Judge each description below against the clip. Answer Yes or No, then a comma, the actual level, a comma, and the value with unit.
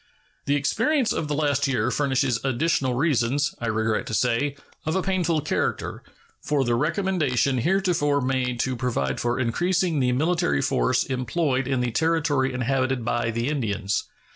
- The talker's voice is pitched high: No, low, 135 Hz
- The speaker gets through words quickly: No, average, 155 wpm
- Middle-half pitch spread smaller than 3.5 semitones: No, average, 4.1 semitones